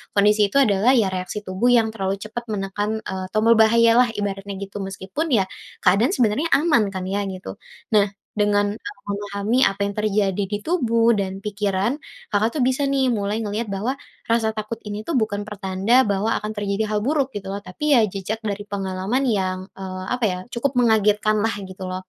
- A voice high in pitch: Yes, high, 210 Hz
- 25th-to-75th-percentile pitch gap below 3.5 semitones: Yes, average, 2.7 semitones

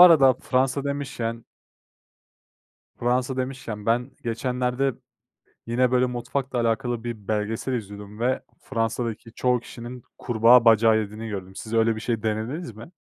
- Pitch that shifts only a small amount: Yes, narrow, 2.2 semitones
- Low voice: Yes, low, 120 Hz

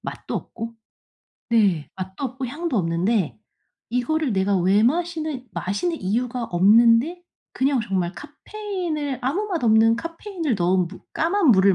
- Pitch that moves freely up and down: Yes, wide, 8.2 semitones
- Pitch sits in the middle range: No, high, 240 Hz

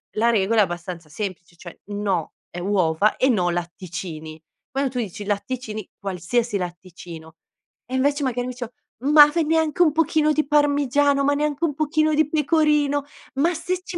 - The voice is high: Yes, high, 245 Hz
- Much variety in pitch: Yes, wide, 8.2 semitones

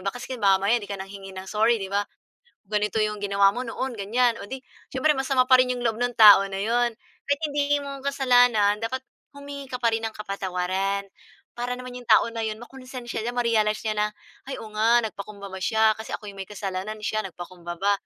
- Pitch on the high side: Yes, high, 220 Hz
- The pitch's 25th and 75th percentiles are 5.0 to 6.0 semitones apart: No, average, 3.8 semitones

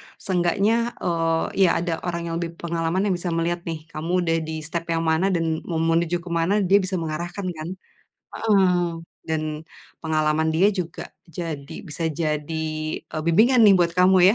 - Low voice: No, medium, 170 Hz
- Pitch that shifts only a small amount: Yes, narrow, 2.1 semitones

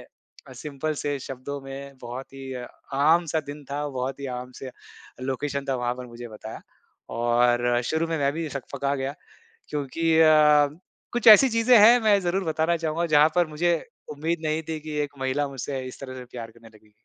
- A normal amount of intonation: Yes, average, 3.4 semitones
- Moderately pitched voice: Yes, medium, 145 Hz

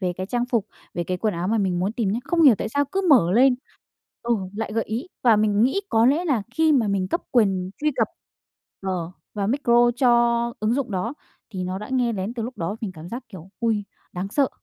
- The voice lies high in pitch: Yes, high, 220 Hz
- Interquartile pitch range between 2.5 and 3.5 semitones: No, average, 4.7 semitones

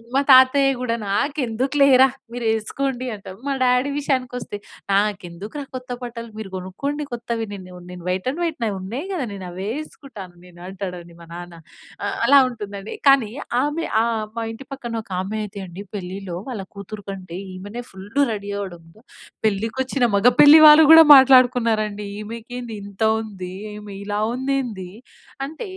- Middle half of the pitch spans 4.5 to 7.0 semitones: Yes, average, 5.1 semitones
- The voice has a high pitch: Yes, high, 225 Hz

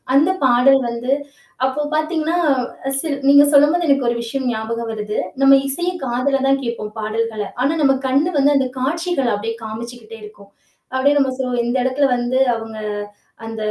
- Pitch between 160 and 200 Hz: No, very high, 260 Hz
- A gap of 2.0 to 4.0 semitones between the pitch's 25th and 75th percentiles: Yes, average, 3.6 semitones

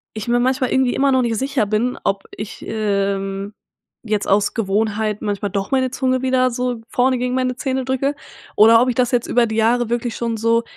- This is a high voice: Yes, high, 235 Hz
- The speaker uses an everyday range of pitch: Yes, average, 3.1 semitones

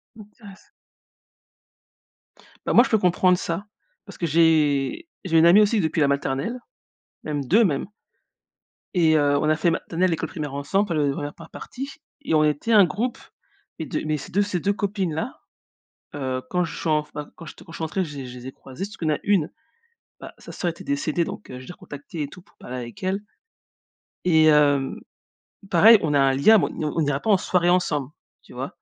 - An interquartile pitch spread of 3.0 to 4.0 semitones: No, average, 4.7 semitones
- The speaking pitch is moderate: Yes, medium, 160 Hz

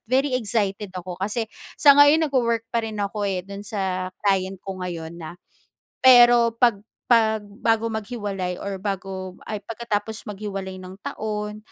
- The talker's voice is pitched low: No, high, 205 Hz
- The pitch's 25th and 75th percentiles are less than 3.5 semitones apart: Yes, average, 3.1 semitones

